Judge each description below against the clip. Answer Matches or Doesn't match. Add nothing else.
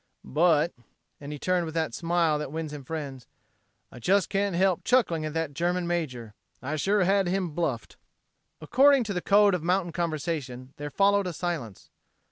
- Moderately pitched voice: Matches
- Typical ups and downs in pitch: Matches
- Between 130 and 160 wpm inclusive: Doesn't match